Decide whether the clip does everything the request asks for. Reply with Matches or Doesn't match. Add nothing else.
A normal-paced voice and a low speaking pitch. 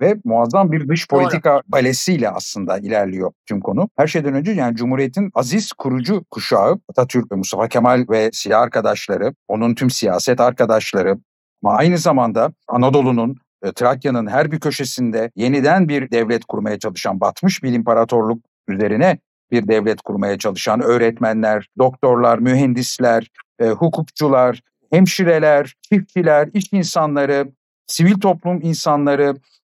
Matches